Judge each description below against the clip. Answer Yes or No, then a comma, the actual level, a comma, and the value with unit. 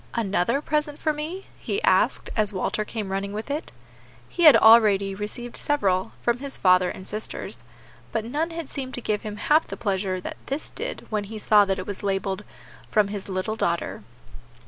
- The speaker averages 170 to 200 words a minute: Yes, average, 190 wpm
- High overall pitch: Yes, high, 215 Hz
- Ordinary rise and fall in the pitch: No, wide, 6.1 semitones